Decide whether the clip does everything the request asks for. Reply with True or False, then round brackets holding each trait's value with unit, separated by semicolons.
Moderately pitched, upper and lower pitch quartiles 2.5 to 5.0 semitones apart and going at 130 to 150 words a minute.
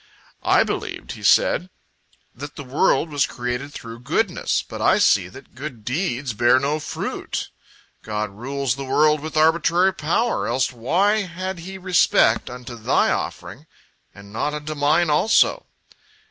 False (145 Hz; 5.4 semitones; 145 wpm)